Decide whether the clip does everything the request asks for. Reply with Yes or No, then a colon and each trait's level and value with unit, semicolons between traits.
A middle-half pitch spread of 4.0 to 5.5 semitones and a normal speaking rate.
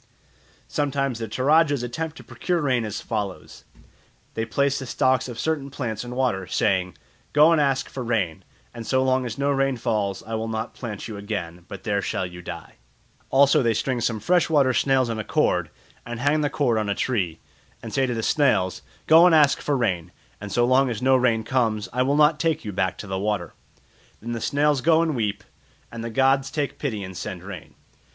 No: average, 4.7 semitones; fast, 210 wpm